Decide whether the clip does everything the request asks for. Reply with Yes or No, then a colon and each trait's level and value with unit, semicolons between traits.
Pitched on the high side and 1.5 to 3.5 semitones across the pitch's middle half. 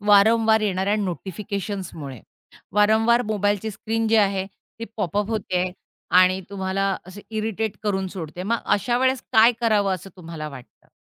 Yes: high, 200 Hz; average, 2.7 semitones